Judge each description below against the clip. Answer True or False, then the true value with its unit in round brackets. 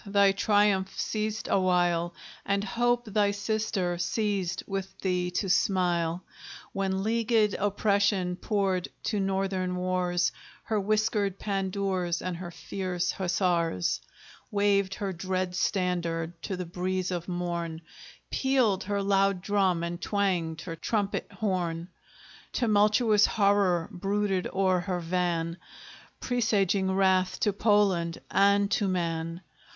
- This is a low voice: False (190 Hz)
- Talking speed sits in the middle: False (120 wpm)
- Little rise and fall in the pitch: True (2.3 semitones)